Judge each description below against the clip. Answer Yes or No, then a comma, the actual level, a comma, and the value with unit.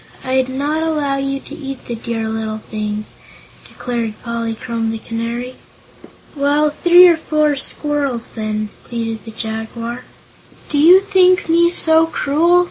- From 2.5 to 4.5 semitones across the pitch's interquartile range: No, average, 5.2 semitones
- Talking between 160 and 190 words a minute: No, slow, 135 wpm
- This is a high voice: Yes, very high, 260 Hz